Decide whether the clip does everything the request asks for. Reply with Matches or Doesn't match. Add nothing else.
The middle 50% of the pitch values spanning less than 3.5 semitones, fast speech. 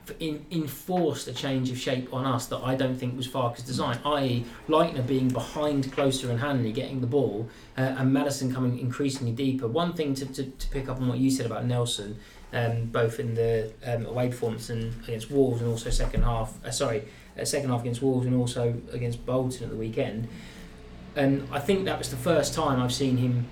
Matches